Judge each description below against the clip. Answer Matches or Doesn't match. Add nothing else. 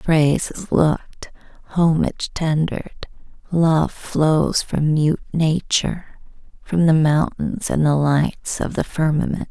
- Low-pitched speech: Doesn't match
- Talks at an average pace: Doesn't match